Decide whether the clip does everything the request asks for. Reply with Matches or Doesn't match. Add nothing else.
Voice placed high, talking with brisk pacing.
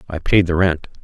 Doesn't match